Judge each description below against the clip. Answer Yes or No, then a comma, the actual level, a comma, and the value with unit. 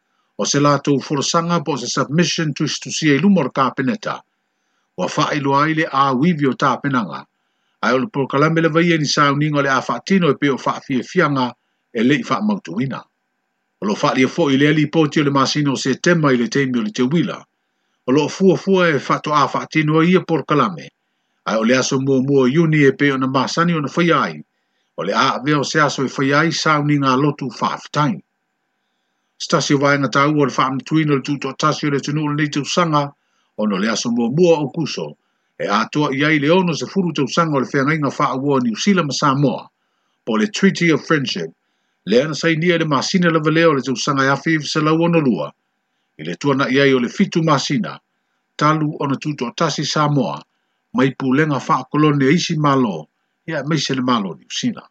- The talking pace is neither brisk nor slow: No, fast, 190 wpm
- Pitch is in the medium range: Yes, medium, 145 Hz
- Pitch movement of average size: Yes, average, 3.3 semitones